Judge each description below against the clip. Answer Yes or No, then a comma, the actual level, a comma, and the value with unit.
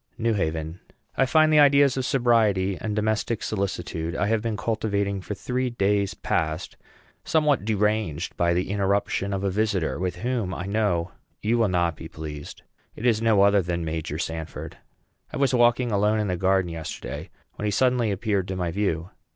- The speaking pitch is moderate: No, low, 100 Hz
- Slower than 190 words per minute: Yes, average, 180 wpm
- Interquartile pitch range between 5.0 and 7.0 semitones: No, average, 4.2 semitones